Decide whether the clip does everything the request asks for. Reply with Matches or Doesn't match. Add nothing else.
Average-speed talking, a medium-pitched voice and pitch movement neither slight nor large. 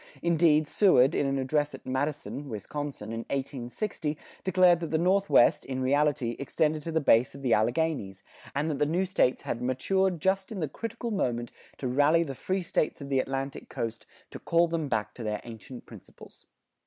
Matches